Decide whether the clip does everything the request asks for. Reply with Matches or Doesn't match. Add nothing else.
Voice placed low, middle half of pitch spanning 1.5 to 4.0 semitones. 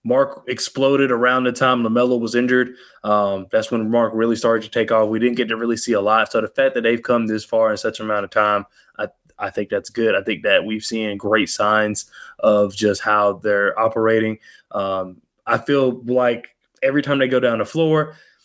Matches